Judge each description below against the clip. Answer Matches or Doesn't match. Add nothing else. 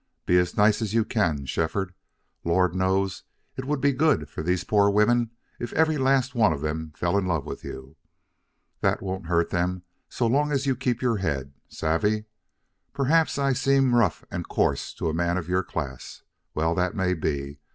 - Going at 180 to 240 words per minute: Matches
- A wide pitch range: Matches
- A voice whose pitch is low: Matches